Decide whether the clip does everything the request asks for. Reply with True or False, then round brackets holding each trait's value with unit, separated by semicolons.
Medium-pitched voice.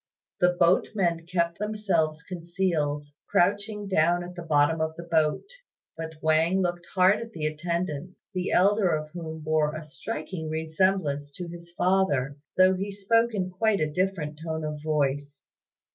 True (170 Hz)